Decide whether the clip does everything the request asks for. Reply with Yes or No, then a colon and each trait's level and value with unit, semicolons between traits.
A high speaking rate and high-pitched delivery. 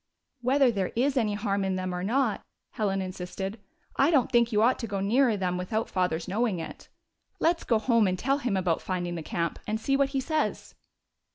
Yes: fast, 215 wpm; high, 215 Hz